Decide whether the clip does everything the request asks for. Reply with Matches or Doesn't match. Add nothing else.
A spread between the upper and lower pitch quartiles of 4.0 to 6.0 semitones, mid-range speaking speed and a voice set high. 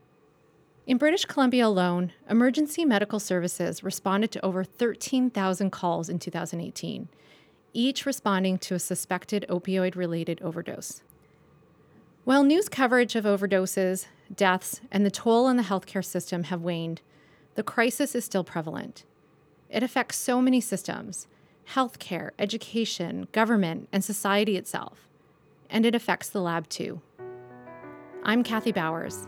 Doesn't match